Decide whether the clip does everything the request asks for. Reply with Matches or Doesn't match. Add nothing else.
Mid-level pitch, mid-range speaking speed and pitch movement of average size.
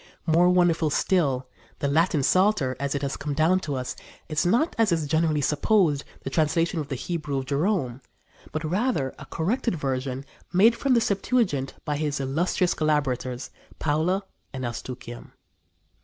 Matches